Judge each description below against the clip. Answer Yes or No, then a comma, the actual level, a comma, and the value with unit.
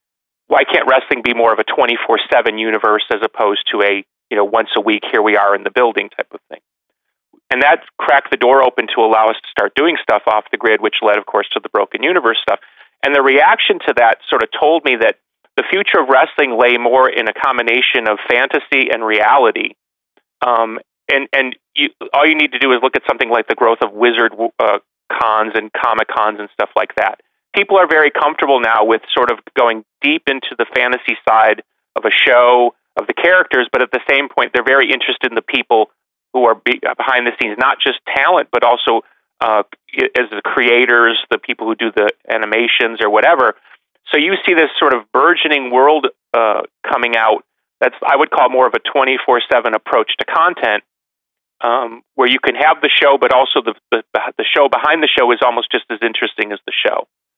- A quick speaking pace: Yes, fast, 215 wpm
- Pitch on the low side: Yes, low, 120 Hz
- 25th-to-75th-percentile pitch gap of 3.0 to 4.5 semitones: Yes, average, 3.4 semitones